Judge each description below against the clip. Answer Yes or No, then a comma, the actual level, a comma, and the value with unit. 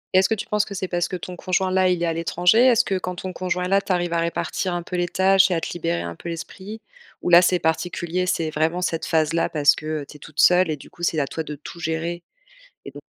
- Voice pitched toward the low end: No, medium, 175 Hz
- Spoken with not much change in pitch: Yes, narrow, 2.3 semitones